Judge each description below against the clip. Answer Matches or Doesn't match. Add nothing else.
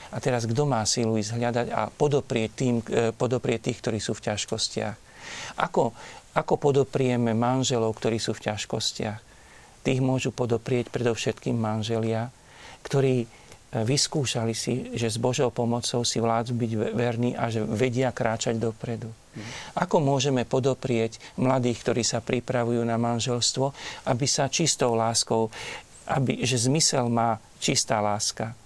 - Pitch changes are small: Matches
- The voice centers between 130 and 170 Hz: Doesn't match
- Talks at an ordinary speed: Matches